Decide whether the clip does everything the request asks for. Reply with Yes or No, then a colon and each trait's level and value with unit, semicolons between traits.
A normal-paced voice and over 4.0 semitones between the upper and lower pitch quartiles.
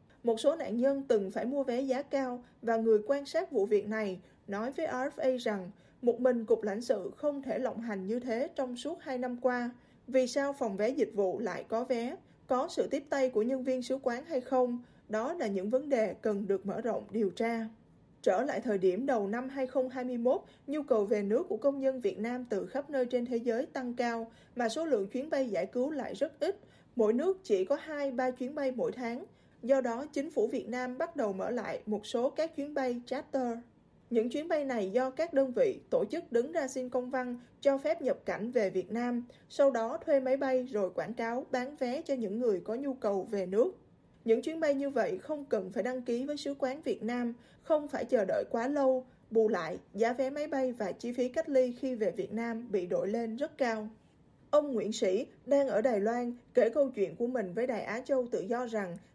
No: average, 230 wpm; average, 3.4 semitones